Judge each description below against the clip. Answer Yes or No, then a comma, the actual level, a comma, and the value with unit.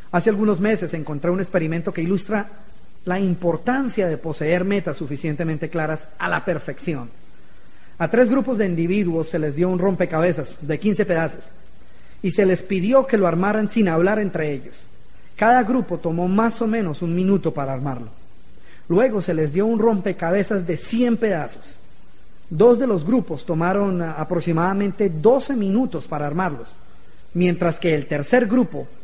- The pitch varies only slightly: No, average, 4.4 semitones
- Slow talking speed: No, average, 155 wpm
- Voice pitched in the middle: Yes, medium, 180 Hz